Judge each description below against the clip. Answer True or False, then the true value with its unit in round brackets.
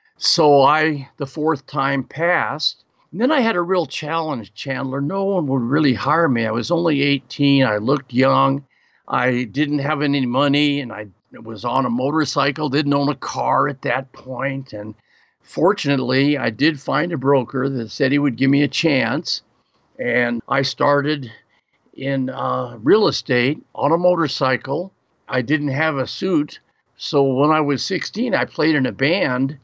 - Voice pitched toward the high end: False (140 Hz)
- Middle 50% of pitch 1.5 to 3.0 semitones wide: True (2.6 semitones)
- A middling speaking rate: True (170 wpm)